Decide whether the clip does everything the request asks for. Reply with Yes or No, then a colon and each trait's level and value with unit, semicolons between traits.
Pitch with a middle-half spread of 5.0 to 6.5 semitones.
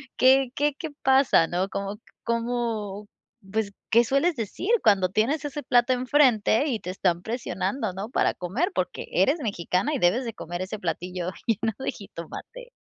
Yes: wide, 5.6 semitones